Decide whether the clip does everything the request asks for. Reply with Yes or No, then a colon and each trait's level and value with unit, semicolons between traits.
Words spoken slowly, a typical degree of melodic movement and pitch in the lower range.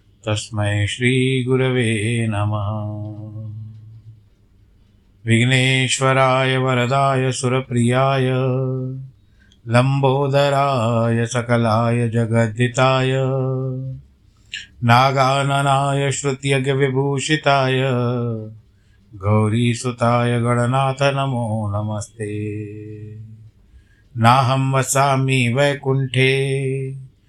Yes: slow, 40 wpm; average, 3.5 semitones; low, 120 Hz